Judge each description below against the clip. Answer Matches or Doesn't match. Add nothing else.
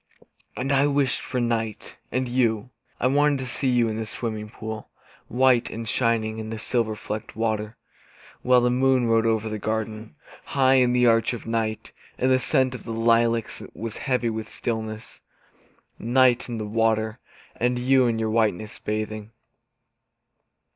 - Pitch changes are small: Matches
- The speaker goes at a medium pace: Matches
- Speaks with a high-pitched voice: Doesn't match